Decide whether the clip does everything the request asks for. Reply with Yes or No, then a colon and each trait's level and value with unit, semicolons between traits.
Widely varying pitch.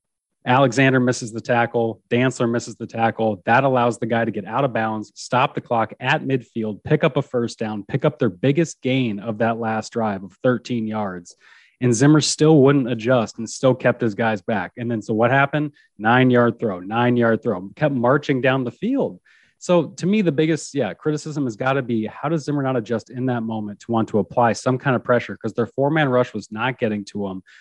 No: average, 3.5 semitones